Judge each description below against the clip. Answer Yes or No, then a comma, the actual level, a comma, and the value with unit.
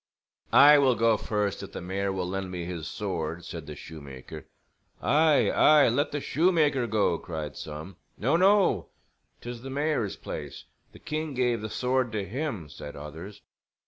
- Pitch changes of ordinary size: No, wide, 8.0 semitones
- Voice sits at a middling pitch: No, low, 105 Hz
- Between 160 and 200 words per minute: Yes, average, 165 wpm